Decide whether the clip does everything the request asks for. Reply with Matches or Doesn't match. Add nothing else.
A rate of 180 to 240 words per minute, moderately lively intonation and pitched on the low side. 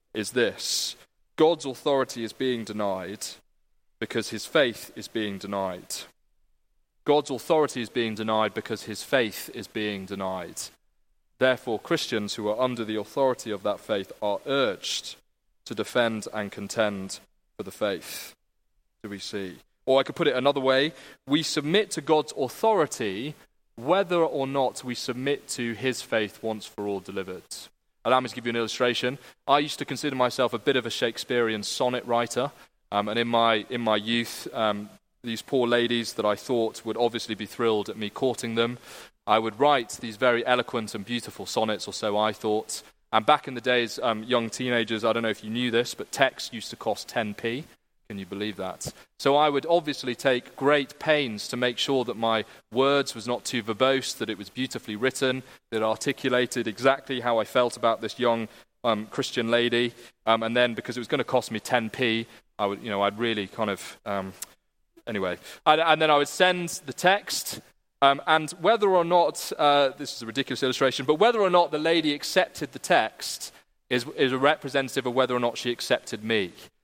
Matches